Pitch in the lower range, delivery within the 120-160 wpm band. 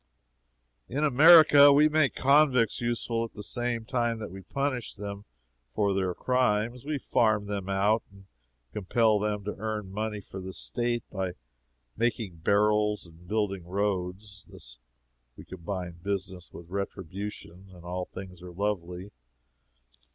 Yes: low, 105 Hz; average, 140 wpm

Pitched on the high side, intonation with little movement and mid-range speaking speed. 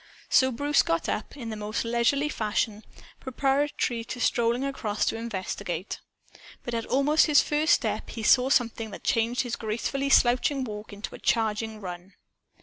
No: high, 235 Hz; average, 3.9 semitones; average, 160 wpm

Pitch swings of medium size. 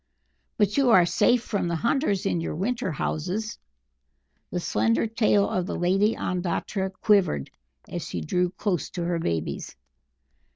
Yes: average, 3.8 semitones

